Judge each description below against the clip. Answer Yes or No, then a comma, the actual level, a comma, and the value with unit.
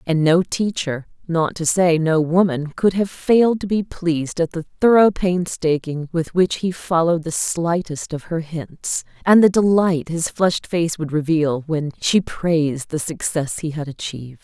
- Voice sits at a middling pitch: Yes, medium, 165 Hz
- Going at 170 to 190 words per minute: Yes, average, 180 wpm